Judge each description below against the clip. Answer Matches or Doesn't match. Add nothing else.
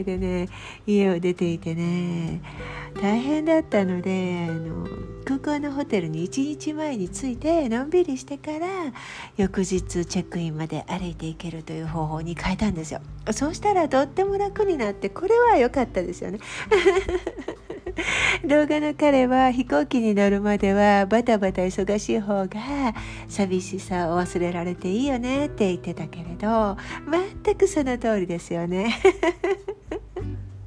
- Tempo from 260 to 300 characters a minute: Matches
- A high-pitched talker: Matches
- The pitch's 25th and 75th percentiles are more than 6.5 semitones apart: Matches